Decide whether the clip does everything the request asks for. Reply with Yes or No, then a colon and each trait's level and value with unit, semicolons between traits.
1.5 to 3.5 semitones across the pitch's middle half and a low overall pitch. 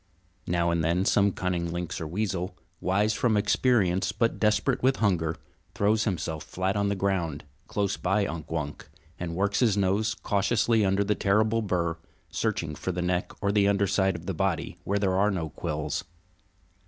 Yes: average, 3.0 semitones; very low, 95 Hz